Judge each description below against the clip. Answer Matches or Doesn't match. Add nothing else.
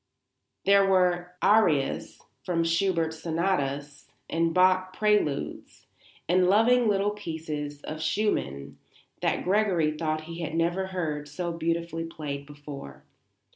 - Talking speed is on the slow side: Matches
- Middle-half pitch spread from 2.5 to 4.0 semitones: Matches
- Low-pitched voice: Doesn't match